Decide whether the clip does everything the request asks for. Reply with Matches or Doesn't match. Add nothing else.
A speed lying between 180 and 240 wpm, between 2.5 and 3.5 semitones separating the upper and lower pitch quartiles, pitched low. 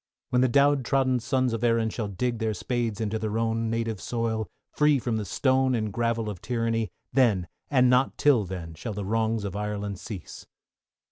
Matches